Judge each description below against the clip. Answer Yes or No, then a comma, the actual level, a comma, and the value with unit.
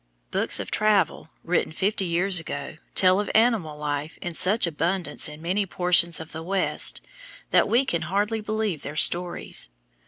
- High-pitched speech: No, medium, 180 Hz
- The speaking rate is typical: Yes, average, 160 wpm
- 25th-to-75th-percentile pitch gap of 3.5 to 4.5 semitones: Yes, average, 4.0 semitones